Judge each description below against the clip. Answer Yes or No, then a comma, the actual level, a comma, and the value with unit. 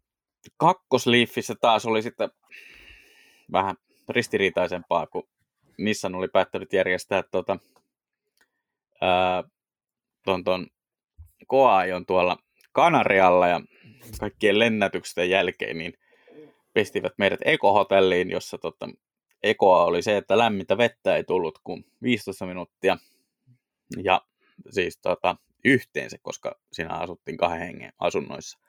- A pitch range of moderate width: Yes, average, 4.2 semitones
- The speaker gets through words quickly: No, slow, 95 wpm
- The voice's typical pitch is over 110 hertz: No, very low, 95 Hz